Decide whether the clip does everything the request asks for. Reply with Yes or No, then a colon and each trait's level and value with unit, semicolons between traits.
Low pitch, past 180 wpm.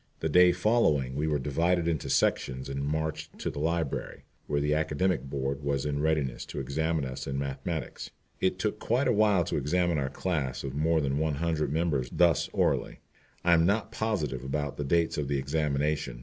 Yes: very low, 75 Hz; average, 190 wpm